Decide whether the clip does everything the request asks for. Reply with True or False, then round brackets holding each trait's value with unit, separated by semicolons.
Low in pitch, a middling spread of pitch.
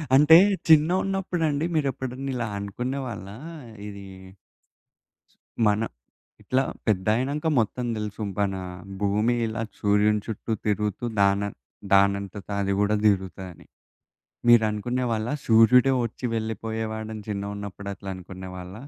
True (110 Hz; 3.5 semitones)